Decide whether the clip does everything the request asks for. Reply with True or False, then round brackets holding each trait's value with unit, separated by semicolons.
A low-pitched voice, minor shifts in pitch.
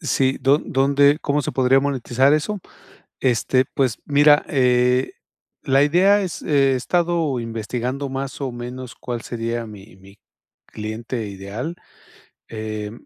False (130 Hz; 3.5 semitones)